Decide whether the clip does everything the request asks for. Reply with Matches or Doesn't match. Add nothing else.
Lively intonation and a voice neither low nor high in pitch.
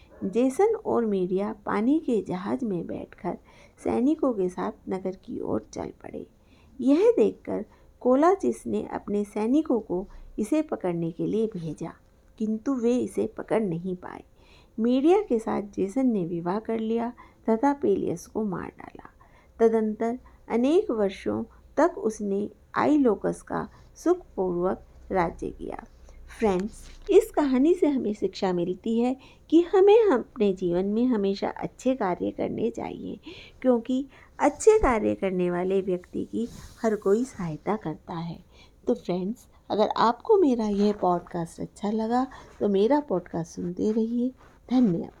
Doesn't match